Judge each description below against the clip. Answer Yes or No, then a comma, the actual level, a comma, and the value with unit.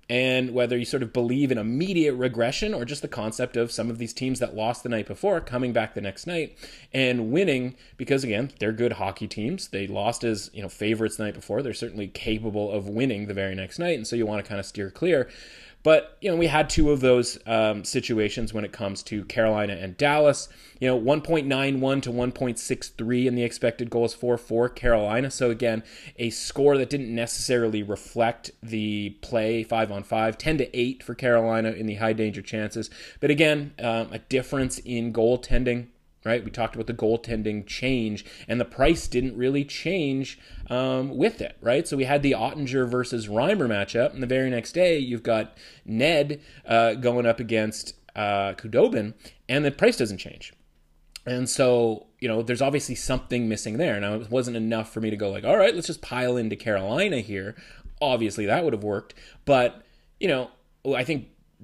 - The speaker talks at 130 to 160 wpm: No, average, 200 wpm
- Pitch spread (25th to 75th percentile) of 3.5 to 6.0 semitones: No, average, 2.9 semitones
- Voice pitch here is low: Yes, low, 120 Hz